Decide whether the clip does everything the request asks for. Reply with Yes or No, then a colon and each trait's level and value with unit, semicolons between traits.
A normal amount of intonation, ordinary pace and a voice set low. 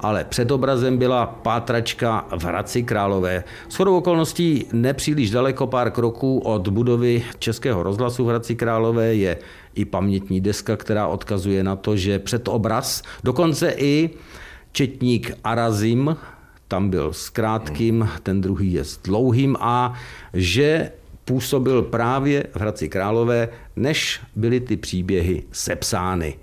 Yes: average, 4.2 semitones; average, 130 wpm; low, 115 Hz